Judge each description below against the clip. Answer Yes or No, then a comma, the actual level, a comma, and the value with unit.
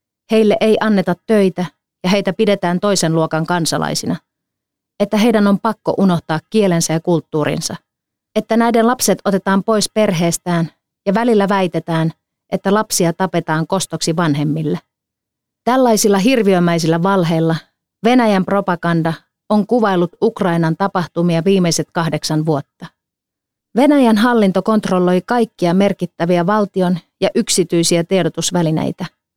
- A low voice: No, medium, 185 Hz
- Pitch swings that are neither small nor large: Yes, average, 4.1 semitones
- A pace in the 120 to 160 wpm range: No, average, 110 wpm